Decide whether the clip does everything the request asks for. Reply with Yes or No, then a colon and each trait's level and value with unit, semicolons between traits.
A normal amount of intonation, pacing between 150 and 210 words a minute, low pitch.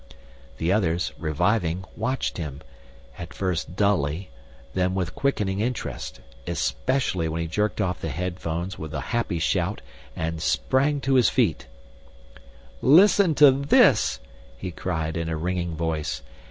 No: average, 4.9 semitones; slow, 135 wpm; very low, 90 Hz